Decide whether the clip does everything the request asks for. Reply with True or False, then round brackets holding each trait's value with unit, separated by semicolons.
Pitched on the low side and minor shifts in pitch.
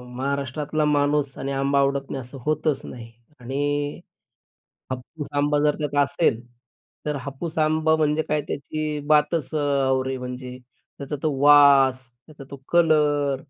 False (145 Hz; 1.9 semitones)